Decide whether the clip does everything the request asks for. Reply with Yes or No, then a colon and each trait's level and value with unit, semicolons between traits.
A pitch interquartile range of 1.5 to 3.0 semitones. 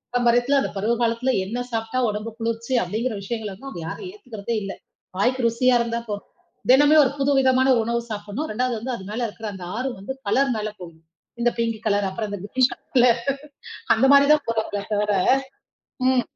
No: average, 3.5 semitones